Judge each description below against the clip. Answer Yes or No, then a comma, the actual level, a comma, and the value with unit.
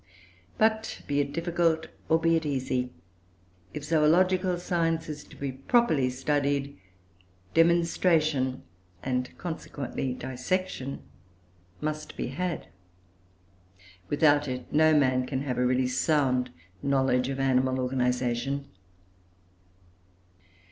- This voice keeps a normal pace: No, slow, 105 wpm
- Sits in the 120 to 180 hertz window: Yes, medium, 140 Hz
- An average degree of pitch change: Yes, average, 4.0 semitones